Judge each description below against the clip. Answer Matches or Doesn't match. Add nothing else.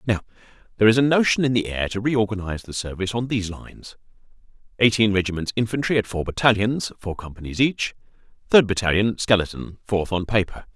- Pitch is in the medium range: Doesn't match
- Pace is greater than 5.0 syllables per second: Matches